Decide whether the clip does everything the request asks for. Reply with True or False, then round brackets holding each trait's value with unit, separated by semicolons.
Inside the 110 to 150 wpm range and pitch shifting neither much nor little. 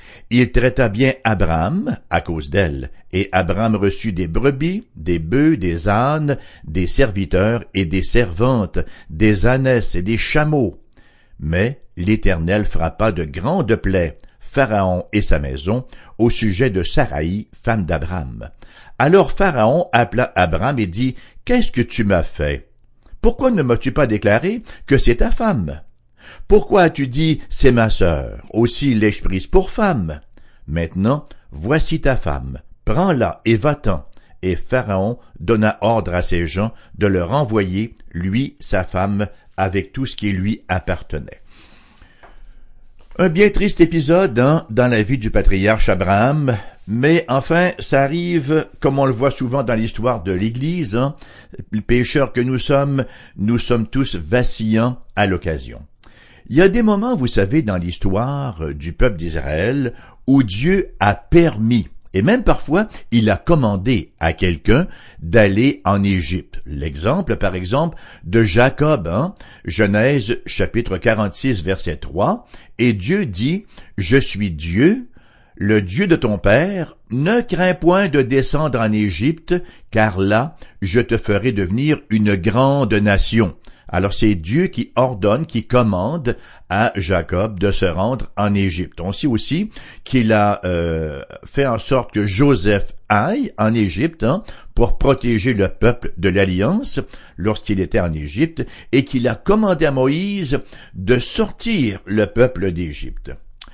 False (145 wpm; 6.0 semitones)